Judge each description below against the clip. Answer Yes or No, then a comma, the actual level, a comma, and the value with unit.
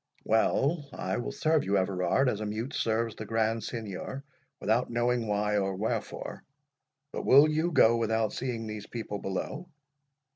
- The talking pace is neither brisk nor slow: Yes, average, 155 wpm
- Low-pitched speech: Yes, low, 115 Hz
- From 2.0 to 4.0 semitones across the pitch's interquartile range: Yes, average, 3.1 semitones